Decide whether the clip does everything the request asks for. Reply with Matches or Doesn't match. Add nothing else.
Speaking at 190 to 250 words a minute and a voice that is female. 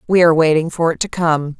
Doesn't match